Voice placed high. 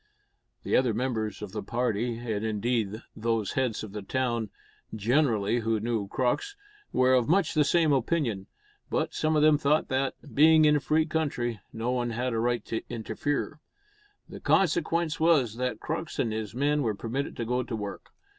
No: low, 120 Hz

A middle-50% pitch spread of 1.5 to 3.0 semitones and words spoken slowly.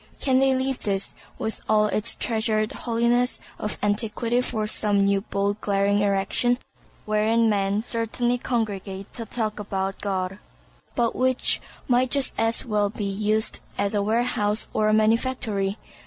No: average, 2.7 semitones; average, 145 wpm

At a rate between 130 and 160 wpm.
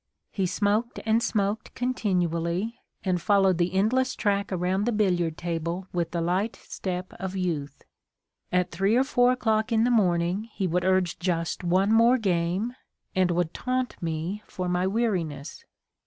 Yes: average, 155 wpm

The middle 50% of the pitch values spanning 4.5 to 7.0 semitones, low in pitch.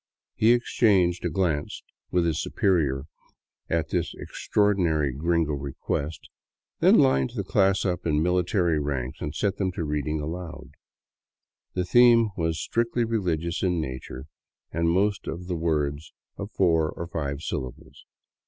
No: average, 3.8 semitones; very low, 85 Hz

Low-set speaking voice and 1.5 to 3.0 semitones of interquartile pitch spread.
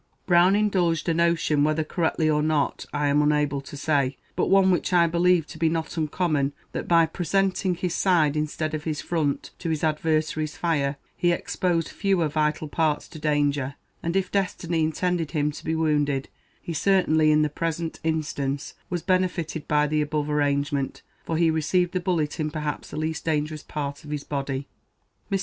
No: medium, 155 Hz; narrow, 2.4 semitones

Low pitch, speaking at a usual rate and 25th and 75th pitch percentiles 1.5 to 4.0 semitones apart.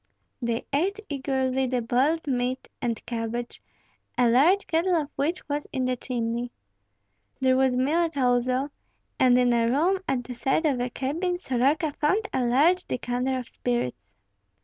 No: very high, 260 Hz; average, 155 wpm; average, 3.4 semitones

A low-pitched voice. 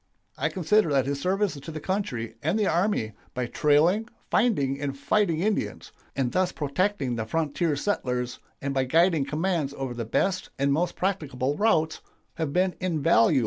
No: medium, 155 Hz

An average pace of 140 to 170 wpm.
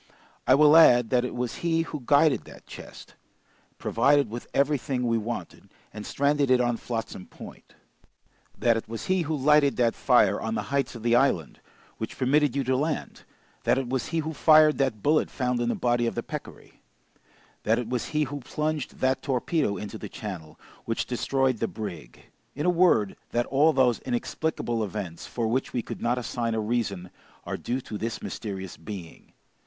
No: average, 190 wpm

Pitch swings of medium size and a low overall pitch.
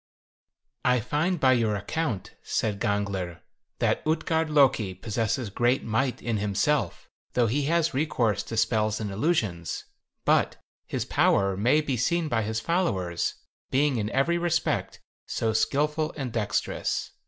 No: wide, 6.2 semitones; low, 120 Hz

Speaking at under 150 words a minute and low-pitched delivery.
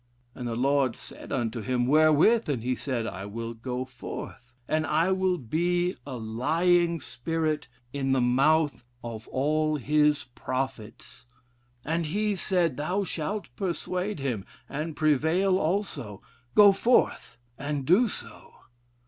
No: slow, 135 wpm; medium, 150 Hz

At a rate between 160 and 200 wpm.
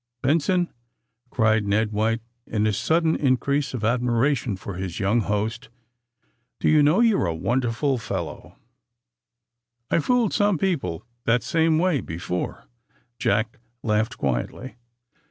No: slow, 135 wpm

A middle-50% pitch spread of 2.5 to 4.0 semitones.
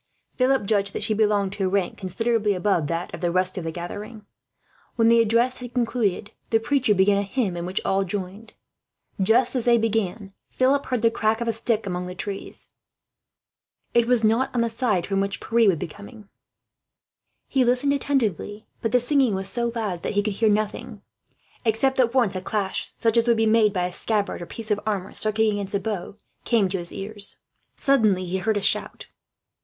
Yes: average, 3.2 semitones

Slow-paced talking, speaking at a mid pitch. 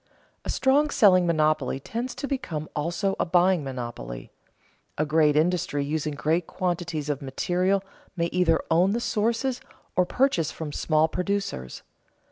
No: average, 145 wpm; medium, 170 Hz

